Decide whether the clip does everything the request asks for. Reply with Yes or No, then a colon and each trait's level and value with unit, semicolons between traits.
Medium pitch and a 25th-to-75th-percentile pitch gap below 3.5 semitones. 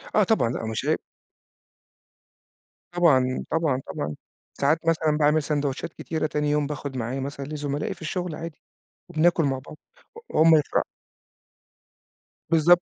Yes: medium, 150 Hz; average, 2.9 semitones